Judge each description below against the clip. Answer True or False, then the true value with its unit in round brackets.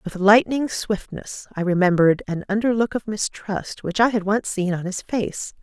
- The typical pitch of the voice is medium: False (200 Hz)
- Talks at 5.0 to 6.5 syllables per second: False (4.7 syllables/s)